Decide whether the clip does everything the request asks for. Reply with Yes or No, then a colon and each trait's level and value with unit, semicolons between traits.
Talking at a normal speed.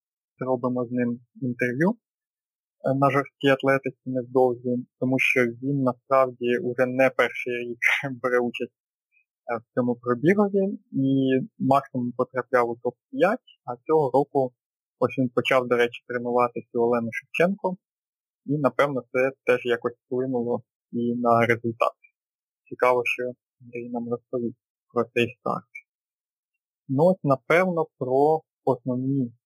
Yes: average, 120 wpm